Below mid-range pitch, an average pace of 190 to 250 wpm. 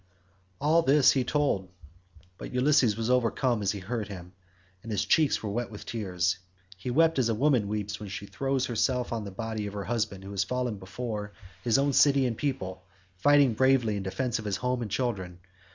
Yes: low, 115 Hz; average, 200 wpm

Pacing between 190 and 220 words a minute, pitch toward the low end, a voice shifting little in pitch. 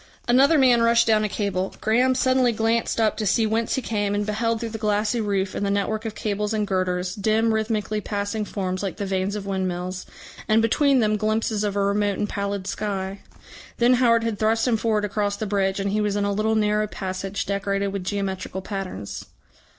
No: fast, 205 wpm; high, 210 Hz; narrow, 2.0 semitones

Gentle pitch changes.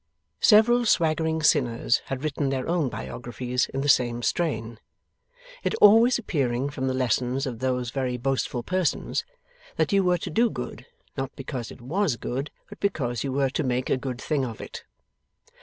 No: average, 4.4 semitones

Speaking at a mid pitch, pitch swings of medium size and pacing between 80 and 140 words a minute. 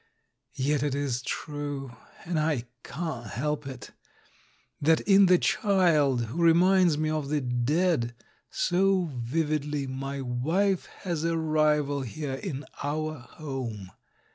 Yes: medium, 150 Hz; average, 3.6 semitones; slow, 135 wpm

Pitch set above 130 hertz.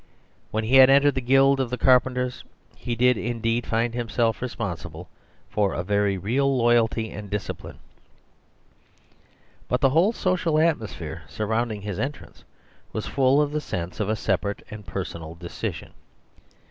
No: low, 115 Hz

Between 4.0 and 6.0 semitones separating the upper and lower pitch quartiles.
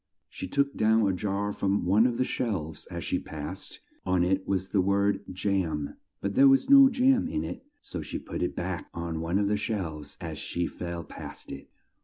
Yes: average, 4.5 semitones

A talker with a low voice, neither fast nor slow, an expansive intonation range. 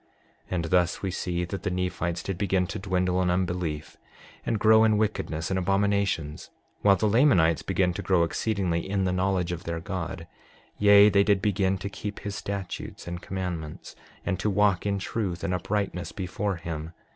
No: very low, 95 Hz; average, 180 wpm; narrow, 2.4 semitones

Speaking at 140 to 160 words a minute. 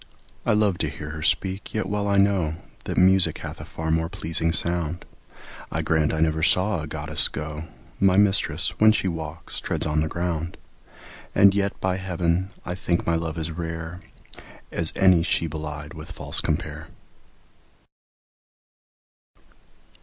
Yes: average, 155 wpm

